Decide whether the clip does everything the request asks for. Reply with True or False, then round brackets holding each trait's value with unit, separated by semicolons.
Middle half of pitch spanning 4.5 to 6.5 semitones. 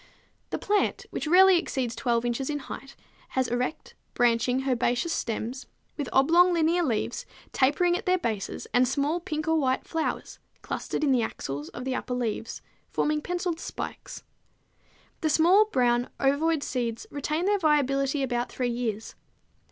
True (4.9 semitones)